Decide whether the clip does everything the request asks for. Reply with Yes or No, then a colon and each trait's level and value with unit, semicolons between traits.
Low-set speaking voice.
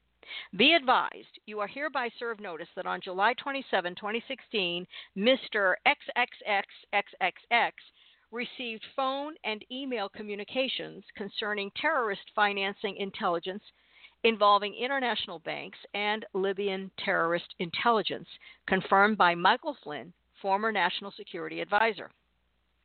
No: high, 205 Hz